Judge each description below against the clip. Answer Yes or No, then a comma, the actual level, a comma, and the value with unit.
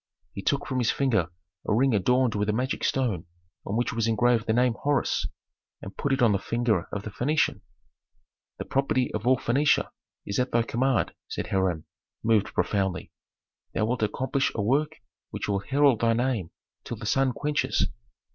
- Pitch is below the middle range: Yes, low, 120 Hz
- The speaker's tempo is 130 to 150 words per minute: No, average, 180 wpm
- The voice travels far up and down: No, average, 4.0 semitones